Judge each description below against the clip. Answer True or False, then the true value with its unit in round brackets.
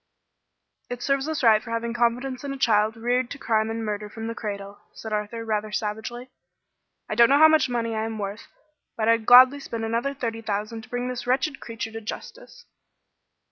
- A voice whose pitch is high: True (230 Hz)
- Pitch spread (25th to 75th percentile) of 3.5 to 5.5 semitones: False (2.5 semitones)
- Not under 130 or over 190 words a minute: False (200 wpm)